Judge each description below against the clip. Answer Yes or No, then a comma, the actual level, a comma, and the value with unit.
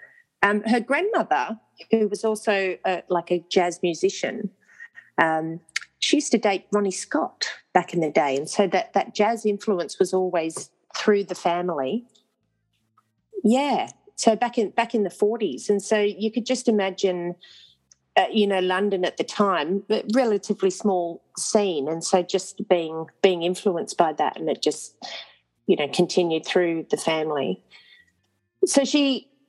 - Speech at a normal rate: Yes, average, 155 wpm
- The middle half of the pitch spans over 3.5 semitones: Yes, average, 4.1 semitones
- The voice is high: Yes, high, 200 Hz